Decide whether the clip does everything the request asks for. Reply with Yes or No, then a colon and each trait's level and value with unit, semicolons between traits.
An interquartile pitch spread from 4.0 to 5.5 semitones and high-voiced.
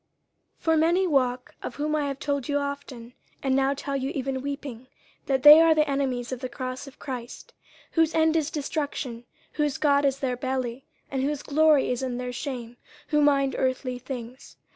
No: narrow, 2.5 semitones; very high, 275 Hz